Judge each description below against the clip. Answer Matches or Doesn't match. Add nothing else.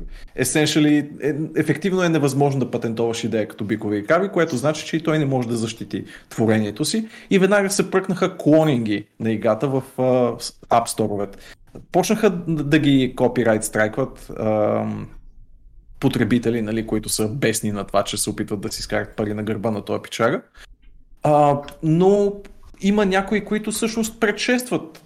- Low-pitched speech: Matches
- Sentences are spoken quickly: Doesn't match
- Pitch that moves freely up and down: Matches